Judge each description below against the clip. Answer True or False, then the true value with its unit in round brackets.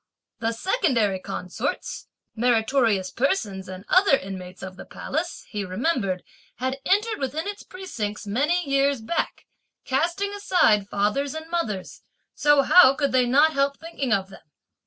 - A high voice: True (265 Hz)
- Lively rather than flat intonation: True (7.6 semitones)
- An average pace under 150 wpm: True (140 wpm)